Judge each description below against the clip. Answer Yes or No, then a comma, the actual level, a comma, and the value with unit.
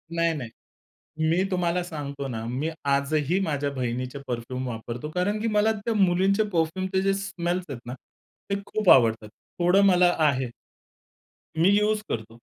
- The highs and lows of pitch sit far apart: Yes, wide, 6.5 semitones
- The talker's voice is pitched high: No, medium, 160 Hz